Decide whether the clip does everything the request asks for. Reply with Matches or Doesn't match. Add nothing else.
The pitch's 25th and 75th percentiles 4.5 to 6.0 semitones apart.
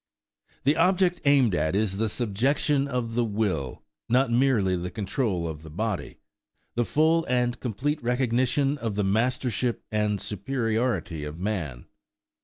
Matches